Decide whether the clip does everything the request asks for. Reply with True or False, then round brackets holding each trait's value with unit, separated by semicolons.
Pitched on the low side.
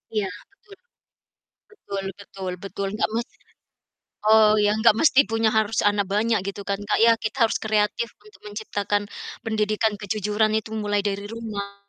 False (210 Hz)